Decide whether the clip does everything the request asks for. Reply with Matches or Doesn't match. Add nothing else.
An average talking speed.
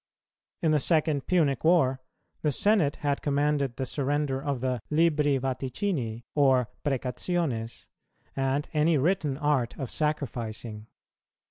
Doesn't match